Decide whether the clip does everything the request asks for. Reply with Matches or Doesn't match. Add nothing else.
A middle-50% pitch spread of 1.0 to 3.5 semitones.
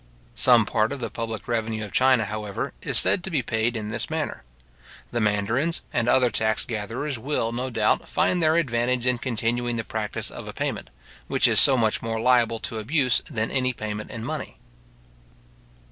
Matches